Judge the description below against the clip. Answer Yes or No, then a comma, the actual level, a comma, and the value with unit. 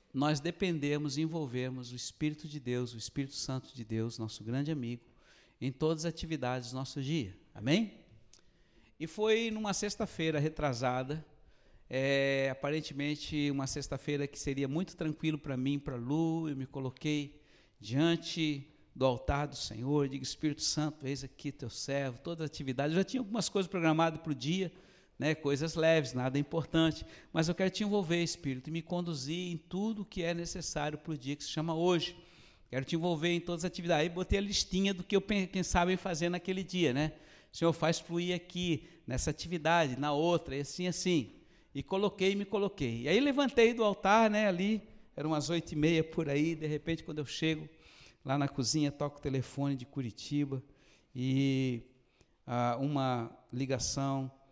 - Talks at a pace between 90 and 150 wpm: No, average, 180 wpm